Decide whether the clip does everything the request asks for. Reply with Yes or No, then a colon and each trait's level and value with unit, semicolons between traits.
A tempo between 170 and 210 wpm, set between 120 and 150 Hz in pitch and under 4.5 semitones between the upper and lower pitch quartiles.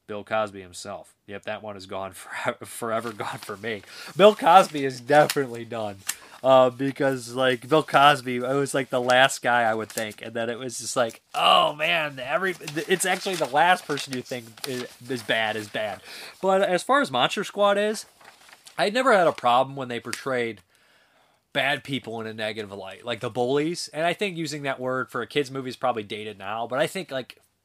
No: fast, 205 wpm; low, 130 Hz; average, 4.9 semitones